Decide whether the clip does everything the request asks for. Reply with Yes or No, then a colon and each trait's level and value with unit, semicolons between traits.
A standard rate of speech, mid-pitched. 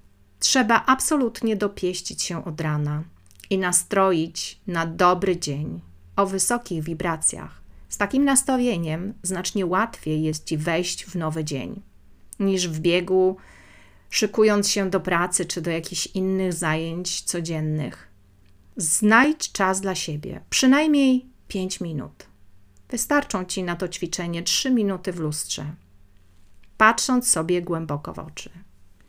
Yes: average, 120 wpm; medium, 175 Hz